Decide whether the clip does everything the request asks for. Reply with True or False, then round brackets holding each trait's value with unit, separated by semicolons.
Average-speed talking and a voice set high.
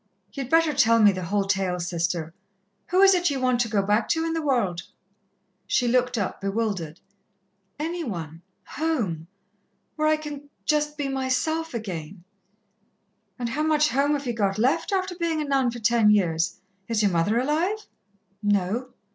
True (170 wpm; 240 Hz)